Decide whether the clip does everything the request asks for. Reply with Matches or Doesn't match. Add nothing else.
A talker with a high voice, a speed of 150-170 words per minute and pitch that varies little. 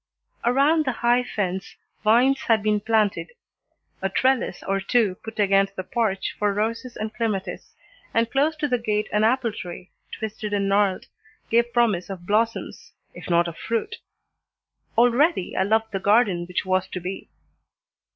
Doesn't match